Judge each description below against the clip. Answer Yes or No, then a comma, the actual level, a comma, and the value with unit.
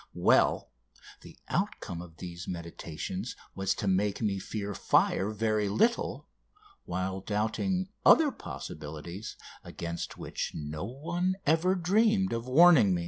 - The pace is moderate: No, slow, 125 wpm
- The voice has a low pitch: Yes, low, 105 Hz